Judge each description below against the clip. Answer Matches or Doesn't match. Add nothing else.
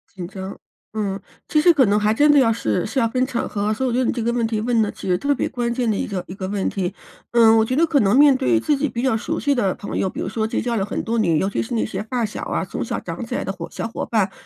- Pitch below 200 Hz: Doesn't match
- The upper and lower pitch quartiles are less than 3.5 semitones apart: Doesn't match